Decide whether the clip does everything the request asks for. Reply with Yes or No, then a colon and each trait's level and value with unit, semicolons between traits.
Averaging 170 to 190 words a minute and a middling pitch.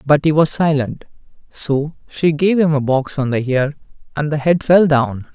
No: average, 200 wpm; medium, 150 Hz